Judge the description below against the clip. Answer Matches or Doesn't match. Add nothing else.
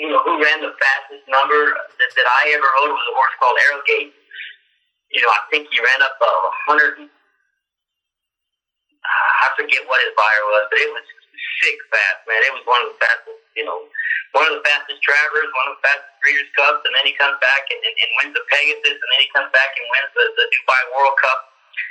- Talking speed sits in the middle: Doesn't match